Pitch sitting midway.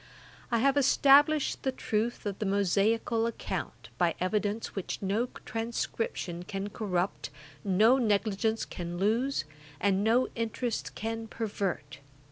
No: high, 220 Hz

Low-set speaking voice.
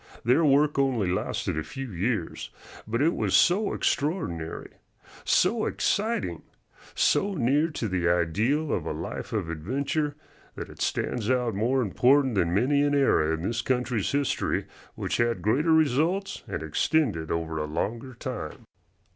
Yes: low, 125 Hz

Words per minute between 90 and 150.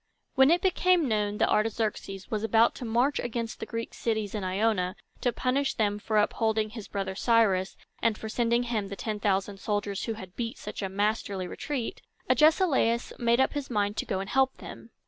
No: average, 195 wpm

